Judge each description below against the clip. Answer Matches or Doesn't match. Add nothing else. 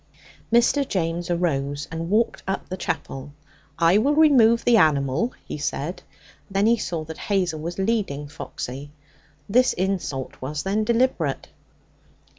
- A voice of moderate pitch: Matches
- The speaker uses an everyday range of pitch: Doesn't match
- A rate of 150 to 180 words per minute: Doesn't match